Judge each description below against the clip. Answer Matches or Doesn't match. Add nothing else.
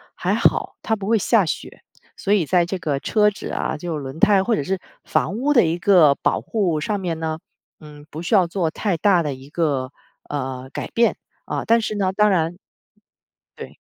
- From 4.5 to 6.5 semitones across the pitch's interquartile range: Matches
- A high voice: Doesn't match